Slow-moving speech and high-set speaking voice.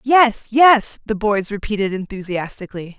Yes: slow, 120 wpm; high, 215 Hz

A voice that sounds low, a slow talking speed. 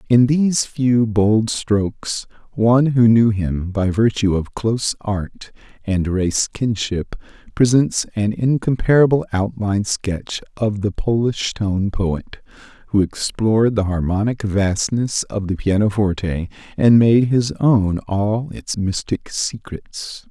Yes: low, 110 Hz; slow, 125 wpm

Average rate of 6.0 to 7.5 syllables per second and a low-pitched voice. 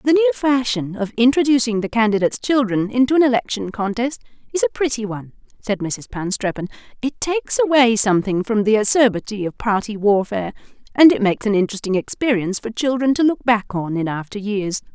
No: 6.1 syllables/s; high, 230 Hz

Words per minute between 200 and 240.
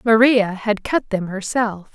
No: average, 155 wpm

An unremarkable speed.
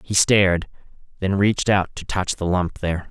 Yes: average, 195 wpm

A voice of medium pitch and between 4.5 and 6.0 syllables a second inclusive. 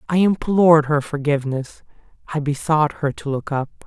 Yes: medium, 150 Hz; 5.0 syllables/s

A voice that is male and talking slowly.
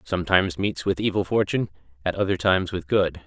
No: male; average, 185 wpm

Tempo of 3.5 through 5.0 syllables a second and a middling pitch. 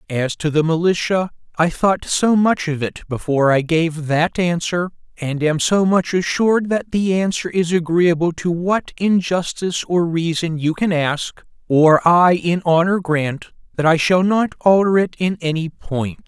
Yes: 4.4 syllables/s; medium, 170 Hz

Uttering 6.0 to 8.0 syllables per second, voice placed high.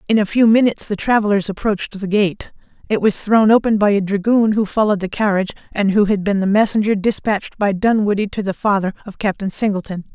Yes: 6.2 syllables/s; high, 205 Hz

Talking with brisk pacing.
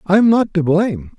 Yes: fast, 255 wpm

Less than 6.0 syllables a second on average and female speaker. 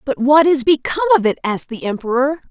No: 6.3 syllables/s; female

